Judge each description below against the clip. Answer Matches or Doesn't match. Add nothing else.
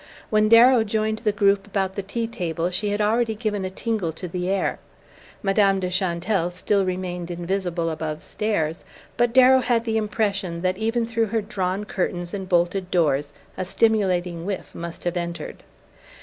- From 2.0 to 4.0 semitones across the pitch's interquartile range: Matches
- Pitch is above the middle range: Matches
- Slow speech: Doesn't match